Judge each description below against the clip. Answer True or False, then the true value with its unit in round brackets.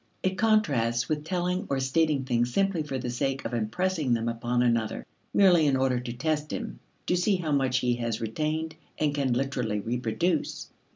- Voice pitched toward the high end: False (135 Hz)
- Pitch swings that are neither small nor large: True (5.0 semitones)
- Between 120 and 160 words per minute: False (180 wpm)